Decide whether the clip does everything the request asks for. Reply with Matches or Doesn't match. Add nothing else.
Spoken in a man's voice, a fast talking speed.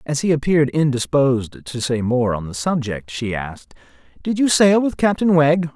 Doesn't match